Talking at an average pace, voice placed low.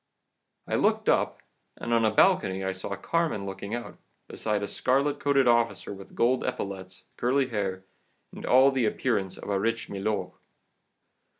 Yes: average, 160 wpm; low, 110 Hz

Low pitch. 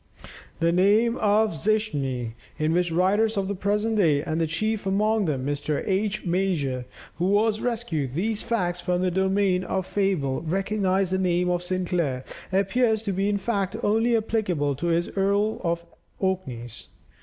No: high, 190 Hz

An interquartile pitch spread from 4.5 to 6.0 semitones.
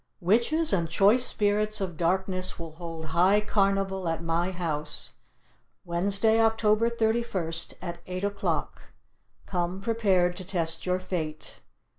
No: average, 3.6 semitones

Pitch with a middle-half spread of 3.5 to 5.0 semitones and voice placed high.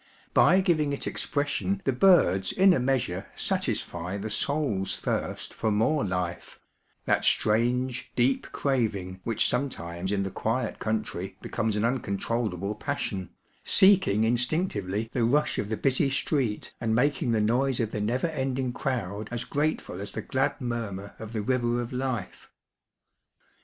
No: average, 4.7 semitones; low, 115 Hz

